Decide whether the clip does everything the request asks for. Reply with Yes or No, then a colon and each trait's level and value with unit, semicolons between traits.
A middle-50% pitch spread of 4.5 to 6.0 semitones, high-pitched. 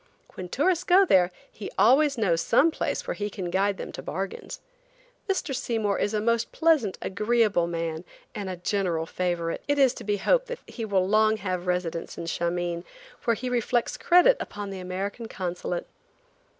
Yes: average, 5.0 semitones; high, 205 Hz